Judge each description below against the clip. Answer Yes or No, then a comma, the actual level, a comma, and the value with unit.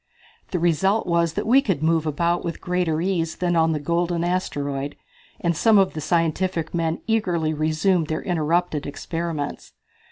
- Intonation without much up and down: Yes, narrow, 2.3 semitones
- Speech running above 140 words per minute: Yes, average, 160 wpm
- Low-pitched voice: No, medium, 170 Hz